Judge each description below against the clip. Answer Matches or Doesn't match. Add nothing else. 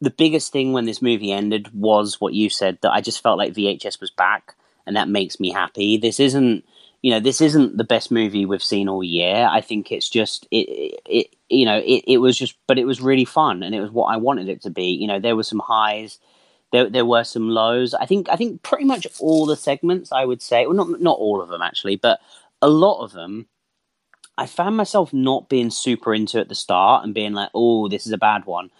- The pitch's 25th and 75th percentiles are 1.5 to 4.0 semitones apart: Doesn't match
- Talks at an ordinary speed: Doesn't match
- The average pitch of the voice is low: Matches